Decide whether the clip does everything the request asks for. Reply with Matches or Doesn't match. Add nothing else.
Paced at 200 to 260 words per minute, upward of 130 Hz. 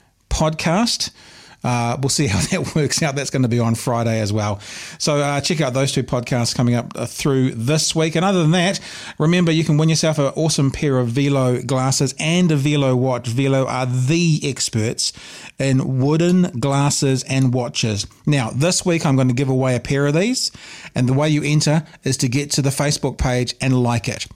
Matches